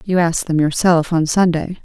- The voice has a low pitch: No, medium, 165 Hz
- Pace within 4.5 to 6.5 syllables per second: Yes, 5.3 syllables/s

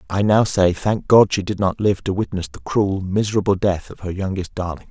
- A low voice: Yes, very low, 95 Hz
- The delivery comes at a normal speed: No, fast, 230 wpm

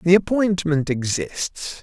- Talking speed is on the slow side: Yes, slow, 100 wpm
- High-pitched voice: No, medium, 165 Hz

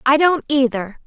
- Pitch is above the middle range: Yes, very high, 265 Hz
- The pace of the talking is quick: No, average, 170 wpm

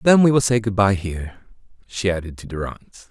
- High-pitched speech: No, low, 100 Hz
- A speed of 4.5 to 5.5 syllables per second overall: No, 5.8 syllables/s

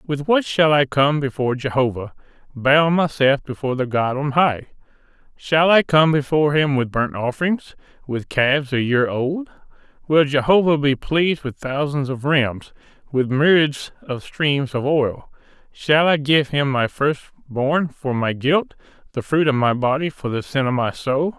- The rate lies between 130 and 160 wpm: No, average, 175 wpm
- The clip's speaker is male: Yes, male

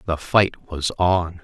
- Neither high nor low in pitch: No, very low, 85 Hz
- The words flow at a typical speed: Yes, average, 165 wpm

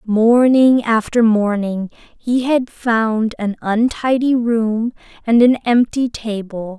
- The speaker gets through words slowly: Yes, slow, 115 wpm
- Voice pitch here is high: Yes, high, 230 Hz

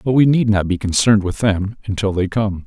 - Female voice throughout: No, male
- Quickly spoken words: Yes, fast, 245 wpm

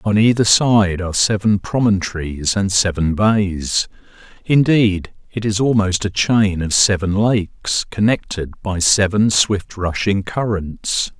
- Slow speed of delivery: Yes, slow, 130 wpm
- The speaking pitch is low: Yes, low, 100 Hz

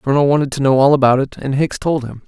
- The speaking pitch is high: No, low, 135 Hz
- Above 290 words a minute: Yes, fast, 315 wpm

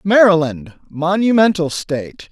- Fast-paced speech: No, slow, 80 wpm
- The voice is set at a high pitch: No, medium, 180 Hz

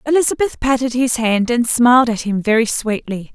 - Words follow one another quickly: No, average, 180 wpm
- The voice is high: Yes, high, 240 Hz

